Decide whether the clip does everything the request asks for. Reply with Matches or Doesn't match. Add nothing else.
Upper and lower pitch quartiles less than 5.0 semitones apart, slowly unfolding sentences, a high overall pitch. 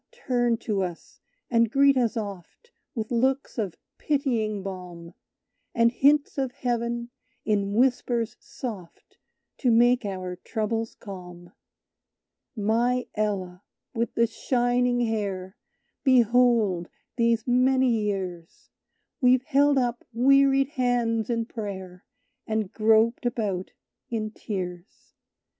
Matches